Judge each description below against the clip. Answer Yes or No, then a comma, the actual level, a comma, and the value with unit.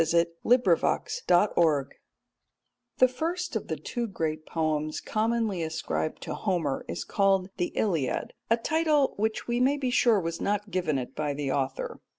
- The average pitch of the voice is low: No, high, 190 Hz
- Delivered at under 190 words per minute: Yes, average, 160 wpm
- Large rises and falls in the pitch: Yes, wide, 7.1 semitones